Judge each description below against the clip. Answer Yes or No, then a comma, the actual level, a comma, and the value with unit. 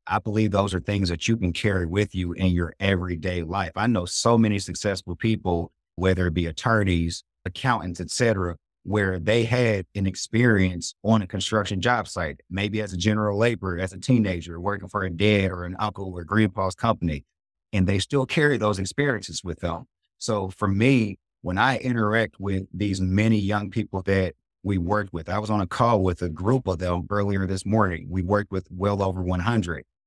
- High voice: No, very low, 95 Hz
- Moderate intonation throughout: Yes, average, 3.1 semitones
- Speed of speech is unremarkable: Yes, average, 195 wpm